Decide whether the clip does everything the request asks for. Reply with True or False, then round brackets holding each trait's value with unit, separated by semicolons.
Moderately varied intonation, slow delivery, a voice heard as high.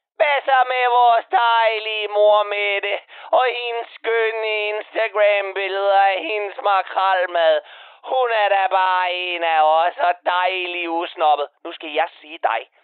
True (3.7 semitones; 130 wpm; 200 Hz)